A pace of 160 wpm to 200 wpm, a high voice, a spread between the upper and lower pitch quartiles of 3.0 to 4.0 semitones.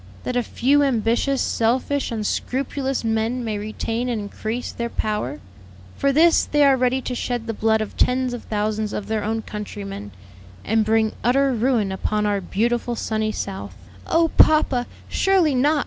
Yes: average, 165 wpm; high, 235 Hz; average, 3.3 semitones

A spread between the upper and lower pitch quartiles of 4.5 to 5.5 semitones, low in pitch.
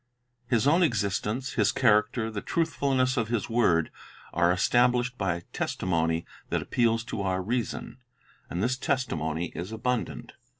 Yes: average, 5.2 semitones; low, 115 Hz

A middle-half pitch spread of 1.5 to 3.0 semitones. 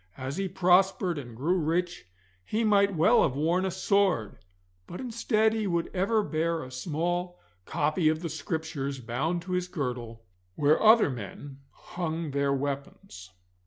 No: average, 5.0 semitones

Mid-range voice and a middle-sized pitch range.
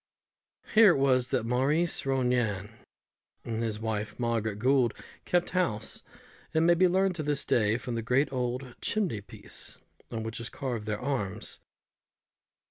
No: low, 125 Hz; average, 4.0 semitones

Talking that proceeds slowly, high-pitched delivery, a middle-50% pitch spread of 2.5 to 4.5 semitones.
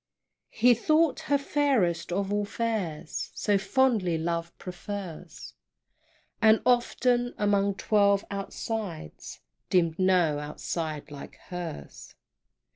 No: slow, 100 wpm; high, 195 Hz; average, 5.0 semitones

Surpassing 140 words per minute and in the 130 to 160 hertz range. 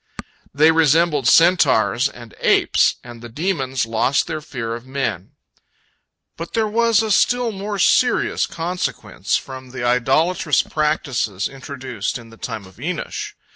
No: slow, 135 wpm; medium, 140 Hz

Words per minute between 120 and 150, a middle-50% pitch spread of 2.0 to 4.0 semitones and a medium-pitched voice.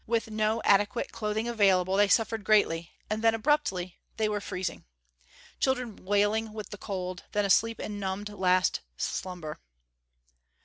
No: average, 140 wpm; average, 2.7 semitones; high, 205 Hz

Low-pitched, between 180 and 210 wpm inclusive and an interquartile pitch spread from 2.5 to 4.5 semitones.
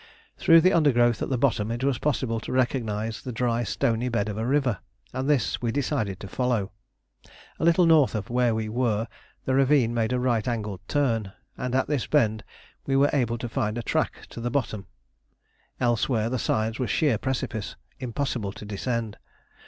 Yes: low, 120 Hz; average, 185 wpm; average, 3.1 semitones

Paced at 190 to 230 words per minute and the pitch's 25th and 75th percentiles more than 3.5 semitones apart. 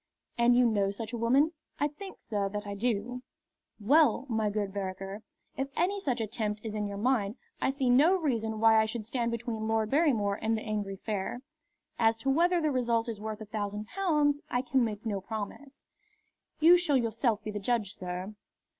Yes: average, 195 wpm; average, 4.0 semitones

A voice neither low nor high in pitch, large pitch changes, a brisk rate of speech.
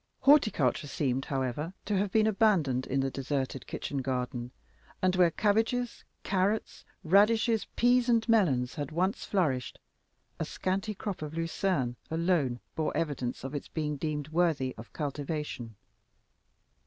No: medium, 160 Hz; wide, 6.9 semitones; slow, 135 wpm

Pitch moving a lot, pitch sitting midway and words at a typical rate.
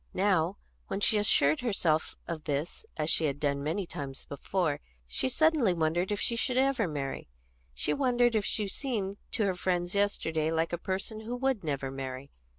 Yes: wide, 6.1 semitones; medium, 180 Hz; average, 185 wpm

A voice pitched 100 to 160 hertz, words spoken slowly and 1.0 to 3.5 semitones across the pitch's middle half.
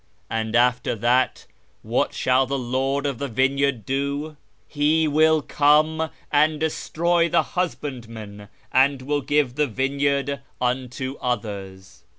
Yes: low, 135 Hz; slow, 125 wpm; average, 3.2 semitones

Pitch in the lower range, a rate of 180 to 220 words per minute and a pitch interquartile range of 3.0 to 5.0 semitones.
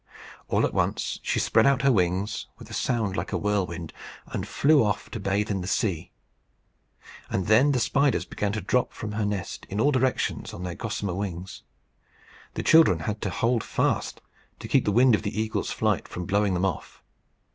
Yes: low, 105 Hz; average, 190 wpm; average, 3.7 semitones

